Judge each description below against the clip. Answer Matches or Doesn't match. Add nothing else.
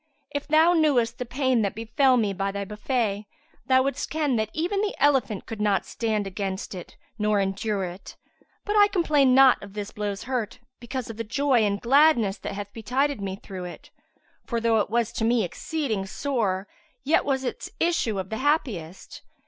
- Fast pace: Doesn't match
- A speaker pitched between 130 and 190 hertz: Doesn't match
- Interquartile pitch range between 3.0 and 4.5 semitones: Doesn't match